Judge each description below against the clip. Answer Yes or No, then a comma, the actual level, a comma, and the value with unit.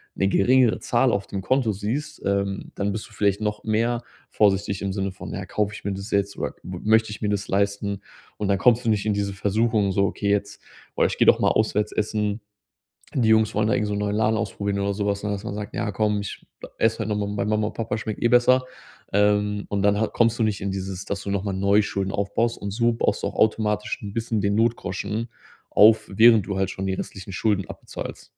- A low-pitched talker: Yes, low, 105 Hz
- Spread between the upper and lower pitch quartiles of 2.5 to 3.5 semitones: No, narrow, 1.8 semitones